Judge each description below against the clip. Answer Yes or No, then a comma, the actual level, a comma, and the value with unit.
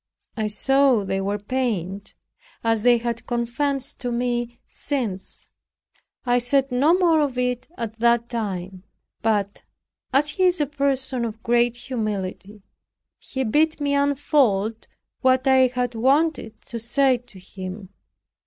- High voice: Yes, high, 240 Hz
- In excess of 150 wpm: No, slow, 135 wpm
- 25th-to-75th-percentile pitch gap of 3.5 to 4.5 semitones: Yes, average, 3.9 semitones